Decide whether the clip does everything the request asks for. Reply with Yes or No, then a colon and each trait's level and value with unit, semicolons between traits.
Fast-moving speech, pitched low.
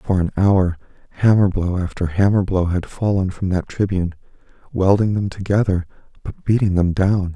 No: average, 165 wpm; very low, 95 Hz